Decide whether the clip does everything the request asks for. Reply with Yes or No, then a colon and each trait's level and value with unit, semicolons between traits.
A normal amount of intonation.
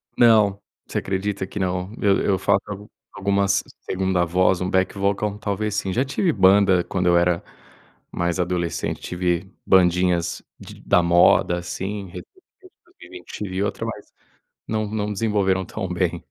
No: narrow, 2.3 semitones